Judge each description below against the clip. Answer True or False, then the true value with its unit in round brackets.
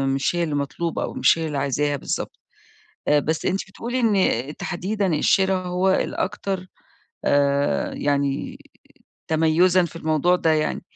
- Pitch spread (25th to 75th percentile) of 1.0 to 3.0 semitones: False (4.2 semitones)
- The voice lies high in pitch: False (165 Hz)